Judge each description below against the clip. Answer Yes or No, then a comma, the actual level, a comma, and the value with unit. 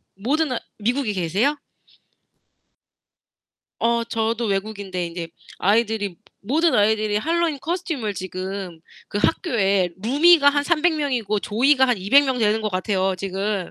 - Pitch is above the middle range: Yes, high, 220 Hz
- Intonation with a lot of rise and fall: Yes, wide, 6.2 semitones